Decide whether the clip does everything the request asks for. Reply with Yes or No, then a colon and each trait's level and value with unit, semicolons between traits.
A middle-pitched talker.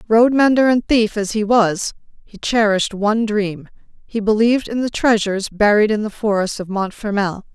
No: high, 215 Hz